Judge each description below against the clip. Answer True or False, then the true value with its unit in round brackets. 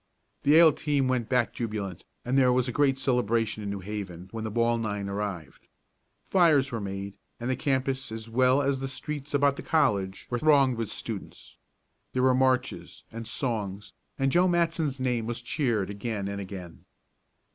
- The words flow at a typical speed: True (180 wpm)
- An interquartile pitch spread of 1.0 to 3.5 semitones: False (4.5 semitones)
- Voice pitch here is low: True (120 Hz)